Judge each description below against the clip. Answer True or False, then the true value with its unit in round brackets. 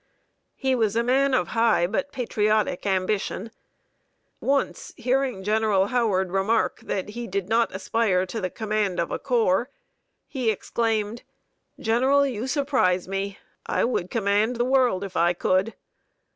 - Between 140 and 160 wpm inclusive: True (145 wpm)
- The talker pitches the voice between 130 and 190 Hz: False (220 Hz)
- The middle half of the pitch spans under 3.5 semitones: False (4.1 semitones)